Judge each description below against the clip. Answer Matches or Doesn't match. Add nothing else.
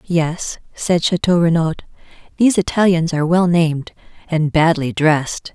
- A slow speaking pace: Matches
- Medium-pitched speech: Matches